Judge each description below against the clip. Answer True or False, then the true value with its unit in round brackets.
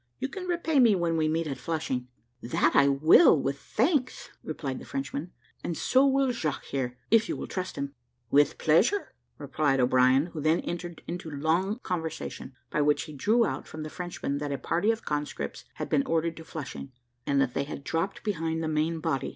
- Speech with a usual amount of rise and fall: True (4.9 semitones)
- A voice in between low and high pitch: True (160 Hz)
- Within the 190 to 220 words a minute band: True (200 wpm)